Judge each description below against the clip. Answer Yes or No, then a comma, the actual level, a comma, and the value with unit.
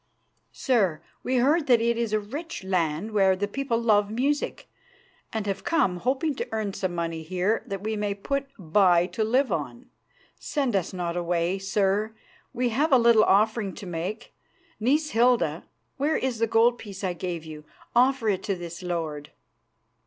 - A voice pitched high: Yes, high, 210 Hz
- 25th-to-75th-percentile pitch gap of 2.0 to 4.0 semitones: No, average, 5.1 semitones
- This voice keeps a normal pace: Yes, average, 175 wpm